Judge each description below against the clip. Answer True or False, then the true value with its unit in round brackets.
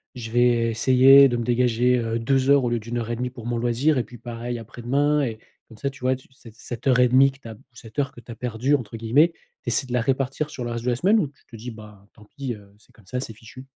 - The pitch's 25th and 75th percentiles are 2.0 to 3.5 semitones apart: True (2.5 semitones)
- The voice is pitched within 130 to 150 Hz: False (120 Hz)